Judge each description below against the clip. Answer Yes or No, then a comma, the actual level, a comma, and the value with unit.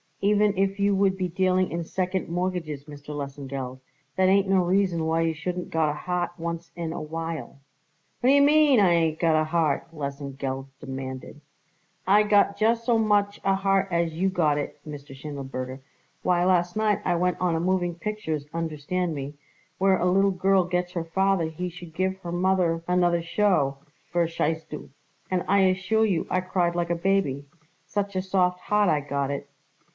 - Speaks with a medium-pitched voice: Yes, medium, 175 Hz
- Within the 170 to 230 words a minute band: Yes, average, 180 wpm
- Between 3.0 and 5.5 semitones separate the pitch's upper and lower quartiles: Yes, average, 3.4 semitones